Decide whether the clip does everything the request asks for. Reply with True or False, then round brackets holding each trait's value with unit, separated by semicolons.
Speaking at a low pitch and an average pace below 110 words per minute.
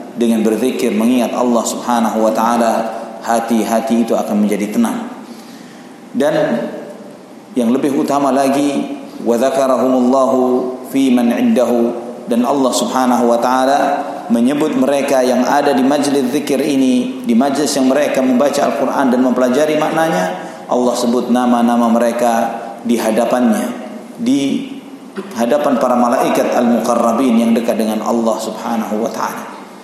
False (125 Hz; 125 wpm)